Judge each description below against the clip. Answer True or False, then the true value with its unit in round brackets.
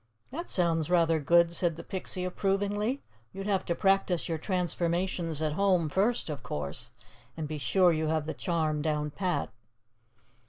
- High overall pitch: False (170 Hz)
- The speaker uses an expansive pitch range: False (3.4 semitones)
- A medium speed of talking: True (165 wpm)